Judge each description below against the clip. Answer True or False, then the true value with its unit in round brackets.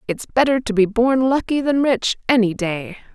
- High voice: True (235 Hz)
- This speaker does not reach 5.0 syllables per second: True (4.7 syllables/s)